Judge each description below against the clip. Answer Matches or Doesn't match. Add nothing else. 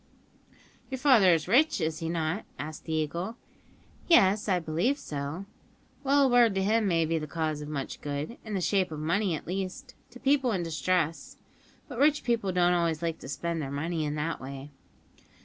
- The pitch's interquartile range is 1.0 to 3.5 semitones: Doesn't match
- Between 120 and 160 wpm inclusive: Doesn't match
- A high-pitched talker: Doesn't match